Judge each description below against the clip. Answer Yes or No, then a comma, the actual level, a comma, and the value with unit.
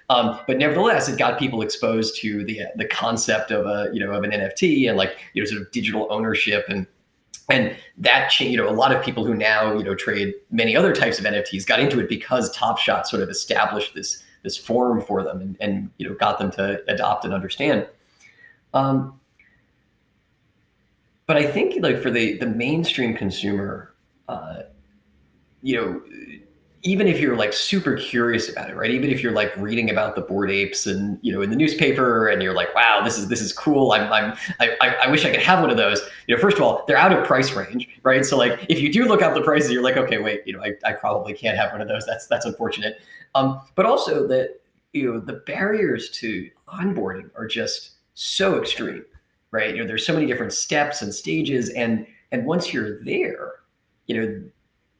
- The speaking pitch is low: Yes, low, 110 Hz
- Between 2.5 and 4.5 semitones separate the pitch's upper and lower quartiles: No, average, 5.0 semitones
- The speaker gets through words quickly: Yes, fast, 215 wpm